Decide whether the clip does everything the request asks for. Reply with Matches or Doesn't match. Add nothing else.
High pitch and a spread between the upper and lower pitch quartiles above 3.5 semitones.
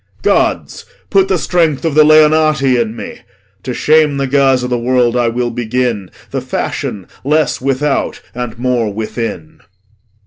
Doesn't match